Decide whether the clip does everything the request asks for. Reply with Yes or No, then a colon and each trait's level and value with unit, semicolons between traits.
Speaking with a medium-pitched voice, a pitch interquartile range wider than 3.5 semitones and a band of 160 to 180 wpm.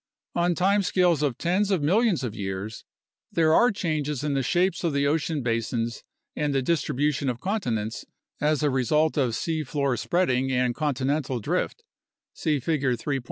Yes: medium, 145 Hz; average, 4.8 semitones; average, 165 wpm